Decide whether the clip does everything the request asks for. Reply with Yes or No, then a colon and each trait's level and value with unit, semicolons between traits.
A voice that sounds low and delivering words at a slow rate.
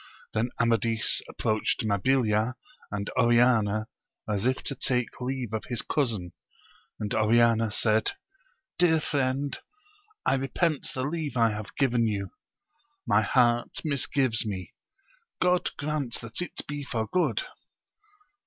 Yes: low, 120 Hz; slow, 125 wpm